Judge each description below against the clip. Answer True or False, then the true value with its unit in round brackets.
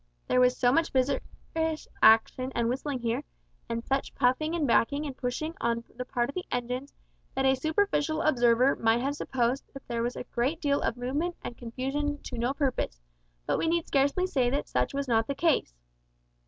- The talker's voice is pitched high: True (265 Hz)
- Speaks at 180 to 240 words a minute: True (190 wpm)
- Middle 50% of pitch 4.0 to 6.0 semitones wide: False (3.3 semitones)